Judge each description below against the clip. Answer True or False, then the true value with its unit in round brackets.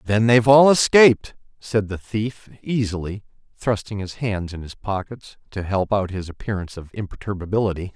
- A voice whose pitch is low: True (105 Hz)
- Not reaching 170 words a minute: True (160 wpm)